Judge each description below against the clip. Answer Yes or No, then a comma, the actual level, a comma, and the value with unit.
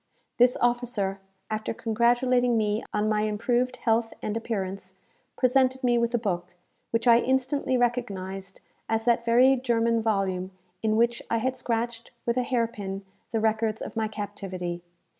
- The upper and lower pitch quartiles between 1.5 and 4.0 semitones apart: Yes, narrow, 2.6 semitones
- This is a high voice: Yes, high, 230 Hz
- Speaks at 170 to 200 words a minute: No, average, 155 wpm